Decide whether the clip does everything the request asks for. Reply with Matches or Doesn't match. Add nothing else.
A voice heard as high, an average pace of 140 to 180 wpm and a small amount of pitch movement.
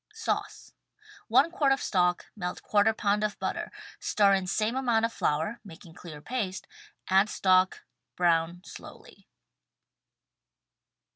Doesn't match